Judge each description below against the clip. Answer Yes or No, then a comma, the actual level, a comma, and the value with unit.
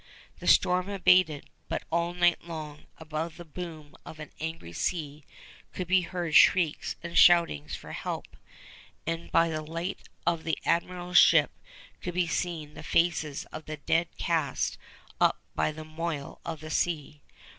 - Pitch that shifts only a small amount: Yes, narrow, 2.1 semitones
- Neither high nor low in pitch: Yes, medium, 165 Hz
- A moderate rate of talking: Yes, average, 155 wpm